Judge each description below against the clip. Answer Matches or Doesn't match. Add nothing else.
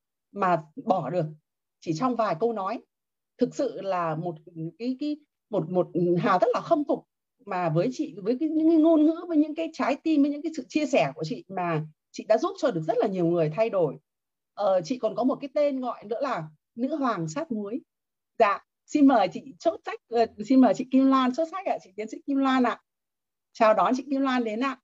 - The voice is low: Doesn't match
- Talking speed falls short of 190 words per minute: Doesn't match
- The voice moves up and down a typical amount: Doesn't match